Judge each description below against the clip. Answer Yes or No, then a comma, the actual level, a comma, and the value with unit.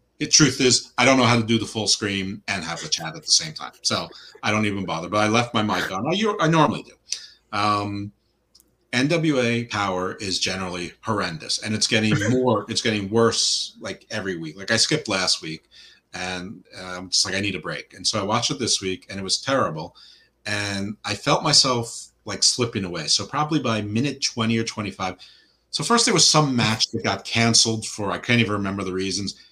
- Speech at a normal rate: No, fast, 215 wpm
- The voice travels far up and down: No, average, 3.7 semitones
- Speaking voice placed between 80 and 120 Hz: Yes, low, 110 Hz